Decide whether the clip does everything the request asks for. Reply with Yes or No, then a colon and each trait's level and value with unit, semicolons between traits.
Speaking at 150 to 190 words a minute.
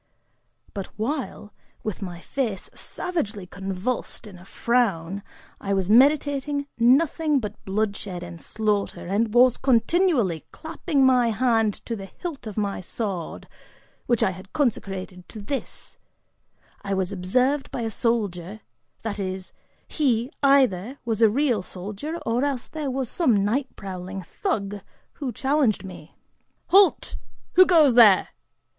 No: slow, 135 wpm